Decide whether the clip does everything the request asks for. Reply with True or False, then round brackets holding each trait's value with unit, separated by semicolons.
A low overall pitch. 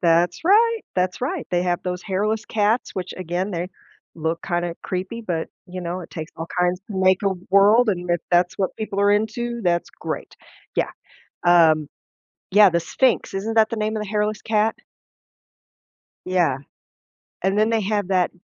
False (190 Hz)